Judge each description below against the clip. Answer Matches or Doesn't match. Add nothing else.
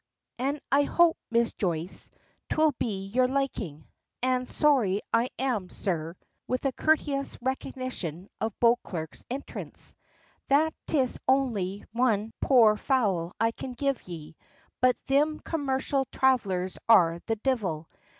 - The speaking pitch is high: Matches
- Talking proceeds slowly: Matches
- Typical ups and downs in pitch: Doesn't match